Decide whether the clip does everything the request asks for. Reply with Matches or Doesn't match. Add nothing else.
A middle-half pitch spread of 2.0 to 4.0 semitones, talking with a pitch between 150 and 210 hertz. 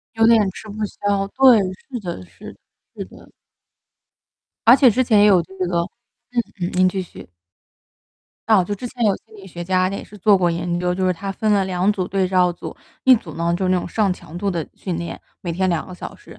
Matches